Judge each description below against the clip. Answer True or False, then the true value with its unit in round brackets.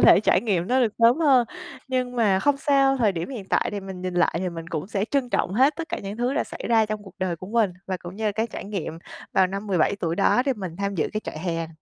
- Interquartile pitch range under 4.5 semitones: False (4.9 semitones)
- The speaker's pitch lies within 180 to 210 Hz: True (205 Hz)